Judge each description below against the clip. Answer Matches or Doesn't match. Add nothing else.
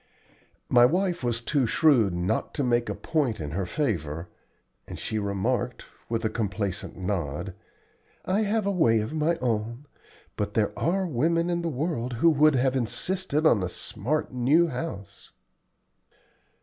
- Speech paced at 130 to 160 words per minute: Matches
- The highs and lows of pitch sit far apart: Matches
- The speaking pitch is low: Matches